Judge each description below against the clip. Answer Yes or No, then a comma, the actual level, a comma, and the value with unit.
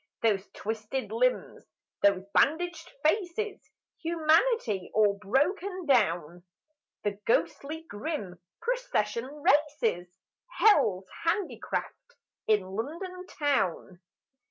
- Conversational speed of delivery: No, slow, 85 wpm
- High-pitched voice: Yes, very high, 285 Hz